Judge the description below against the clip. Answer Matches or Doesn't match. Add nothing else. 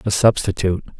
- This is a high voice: Doesn't match